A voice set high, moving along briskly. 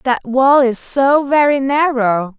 No: very high, 260 Hz; average, 150 wpm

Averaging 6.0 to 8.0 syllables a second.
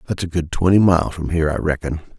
Yes: 7.0 syllables/s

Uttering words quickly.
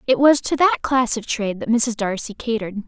Yes: fast, 230 wpm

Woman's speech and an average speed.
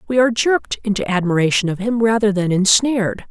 Yes: female; average, 180 wpm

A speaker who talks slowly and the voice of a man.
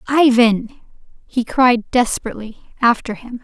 No: slow, 105 wpm; female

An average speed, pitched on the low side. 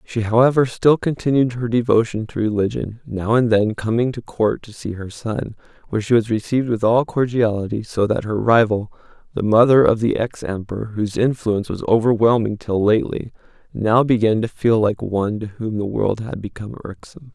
Yes: average, 185 wpm; low, 110 Hz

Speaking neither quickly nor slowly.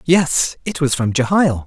Yes: average, 180 wpm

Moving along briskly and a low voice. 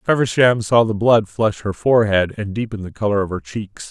Yes: fast, 215 wpm; low, 110 Hz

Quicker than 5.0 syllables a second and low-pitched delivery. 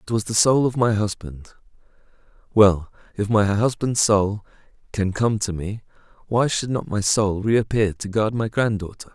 No: 4.5 syllables/s; low, 105 Hz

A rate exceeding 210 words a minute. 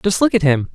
Yes: fast, 325 wpm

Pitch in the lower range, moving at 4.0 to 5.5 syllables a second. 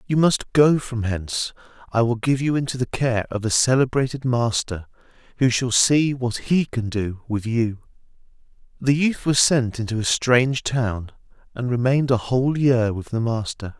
Yes: low, 120 Hz; 4.7 syllables/s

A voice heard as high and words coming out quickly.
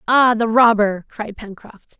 No: high, 220 Hz; average, 150 wpm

